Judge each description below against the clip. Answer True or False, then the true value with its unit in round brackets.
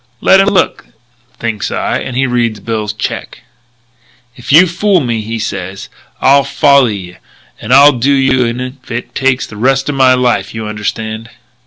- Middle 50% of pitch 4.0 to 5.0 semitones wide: False (3.6 semitones)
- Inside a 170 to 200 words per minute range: True (175 wpm)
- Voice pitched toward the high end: False (125 Hz)